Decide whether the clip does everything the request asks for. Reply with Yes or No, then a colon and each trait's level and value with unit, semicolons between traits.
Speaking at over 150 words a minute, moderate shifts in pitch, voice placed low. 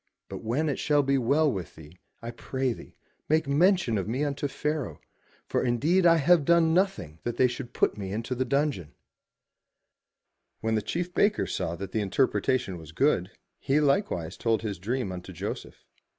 No: average, 180 wpm; wide, 6.3 semitones; low, 130 Hz